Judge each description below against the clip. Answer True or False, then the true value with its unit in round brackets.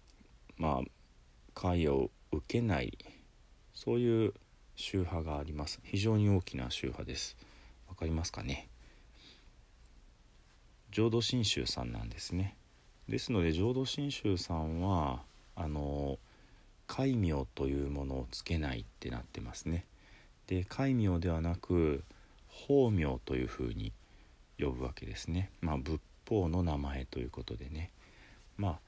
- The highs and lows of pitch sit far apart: True (6.4 semitones)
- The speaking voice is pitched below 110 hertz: True (85 Hz)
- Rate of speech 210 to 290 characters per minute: True (245 characters per minute)